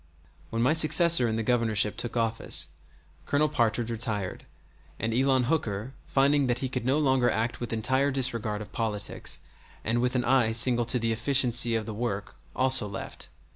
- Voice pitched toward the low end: Yes, low, 120 Hz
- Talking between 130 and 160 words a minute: No, average, 175 wpm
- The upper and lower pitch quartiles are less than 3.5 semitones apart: Yes, average, 2.8 semitones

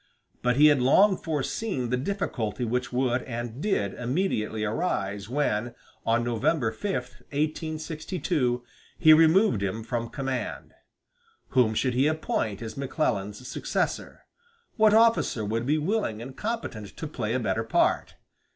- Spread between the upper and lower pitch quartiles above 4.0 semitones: Yes, wide, 5.6 semitones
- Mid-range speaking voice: No, low, 125 Hz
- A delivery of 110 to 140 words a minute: Yes, slow, 135 wpm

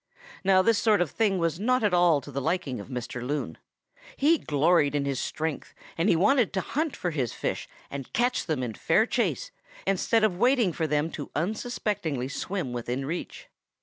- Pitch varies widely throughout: Yes, wide, 6.8 semitones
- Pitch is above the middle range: No, medium, 170 Hz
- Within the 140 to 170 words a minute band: No, average, 190 wpm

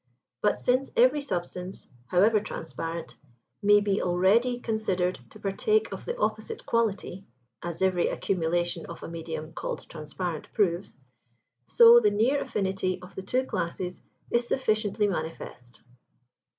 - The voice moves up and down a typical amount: Yes, average, 4.2 semitones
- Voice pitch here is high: Yes, high, 195 Hz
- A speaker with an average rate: No, slow, 130 wpm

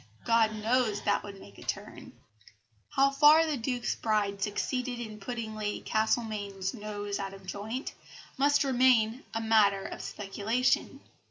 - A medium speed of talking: Yes, average, 150 wpm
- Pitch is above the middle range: Yes, high, 220 Hz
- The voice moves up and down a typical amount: Yes, average, 3.5 semitones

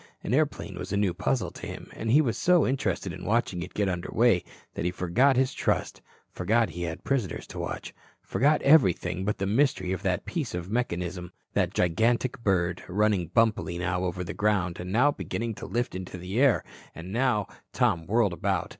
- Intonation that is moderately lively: Yes, average, 5.0 semitones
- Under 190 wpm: No, average, 200 wpm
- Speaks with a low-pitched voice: Yes, low, 100 Hz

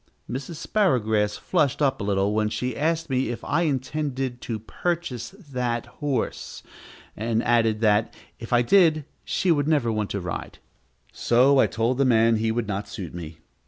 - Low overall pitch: Yes, low, 120 Hz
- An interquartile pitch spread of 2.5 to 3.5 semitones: No, average, 4.8 semitones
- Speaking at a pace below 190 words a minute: Yes, average, 170 wpm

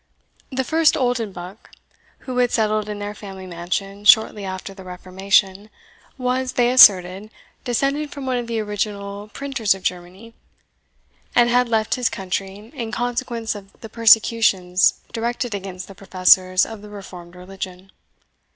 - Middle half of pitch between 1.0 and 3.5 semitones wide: No, average, 3.9 semitones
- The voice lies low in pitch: No, high, 210 Hz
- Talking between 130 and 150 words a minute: Yes, average, 140 wpm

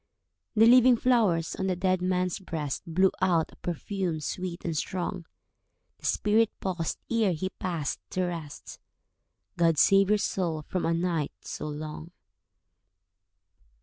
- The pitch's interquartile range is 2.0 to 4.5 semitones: Yes, average, 2.8 semitones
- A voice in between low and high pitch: Yes, medium, 180 Hz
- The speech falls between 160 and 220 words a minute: No, average, 140 wpm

